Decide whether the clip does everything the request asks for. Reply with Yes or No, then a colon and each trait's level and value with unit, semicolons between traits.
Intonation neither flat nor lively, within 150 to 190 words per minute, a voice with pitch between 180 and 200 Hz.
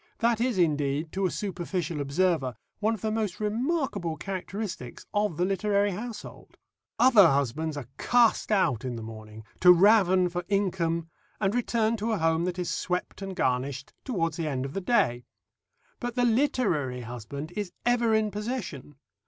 No: wide, 6.2 semitones; average, 165 wpm; medium, 185 Hz